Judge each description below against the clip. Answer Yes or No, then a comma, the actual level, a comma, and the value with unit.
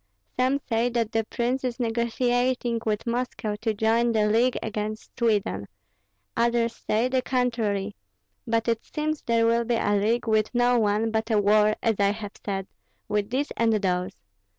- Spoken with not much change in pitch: Yes, narrow, 2.3 semitones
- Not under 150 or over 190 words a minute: Yes, average, 170 wpm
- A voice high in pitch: Yes, high, 225 Hz